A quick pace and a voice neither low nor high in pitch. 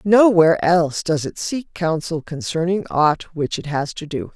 No: average, 180 wpm; medium, 165 Hz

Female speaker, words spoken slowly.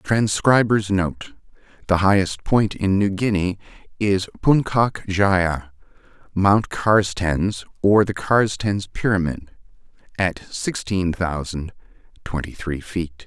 No: male; slow, 105 wpm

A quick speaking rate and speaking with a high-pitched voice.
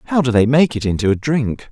No: fast, 280 wpm; low, 125 Hz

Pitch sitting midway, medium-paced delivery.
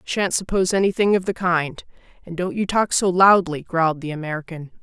Yes: medium, 175 Hz; average, 185 wpm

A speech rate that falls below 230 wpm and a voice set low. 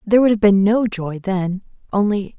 No: average, 200 wpm; high, 200 Hz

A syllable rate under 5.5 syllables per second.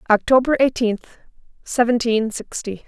Yes: 4.6 syllables/s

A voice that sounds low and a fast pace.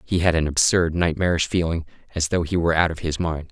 Yes: very low, 85 Hz; fast, 240 wpm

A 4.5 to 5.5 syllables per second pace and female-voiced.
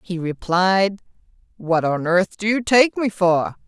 No: 3.7 syllables/s; female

